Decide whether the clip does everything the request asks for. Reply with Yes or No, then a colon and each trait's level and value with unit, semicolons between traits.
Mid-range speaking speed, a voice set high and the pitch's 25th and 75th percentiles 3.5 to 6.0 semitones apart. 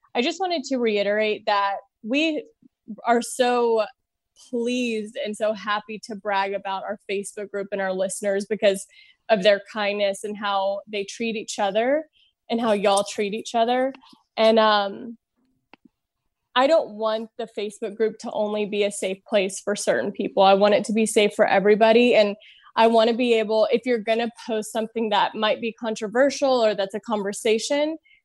No: average, 175 wpm; high, 220 Hz; narrow, 2.6 semitones